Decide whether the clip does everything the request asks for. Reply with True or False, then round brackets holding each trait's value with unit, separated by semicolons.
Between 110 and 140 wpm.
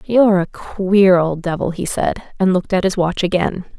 False (205 wpm)